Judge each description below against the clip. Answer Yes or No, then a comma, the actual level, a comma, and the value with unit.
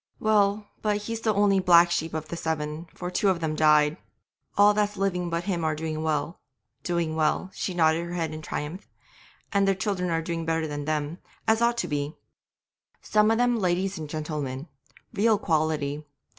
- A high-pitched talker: No, medium, 170 Hz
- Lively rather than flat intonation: No, average, 4.2 semitones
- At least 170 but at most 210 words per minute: Yes, average, 185 wpm